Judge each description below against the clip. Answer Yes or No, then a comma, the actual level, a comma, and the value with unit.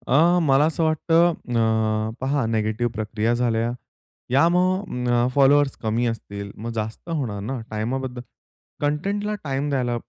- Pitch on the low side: Yes, low, 125 Hz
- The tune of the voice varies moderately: Yes, average, 4.8 semitones